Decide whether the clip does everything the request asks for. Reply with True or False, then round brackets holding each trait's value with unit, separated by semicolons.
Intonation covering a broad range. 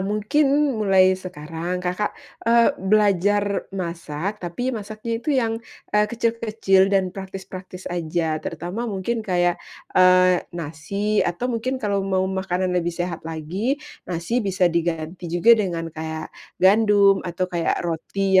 False (3.2 semitones)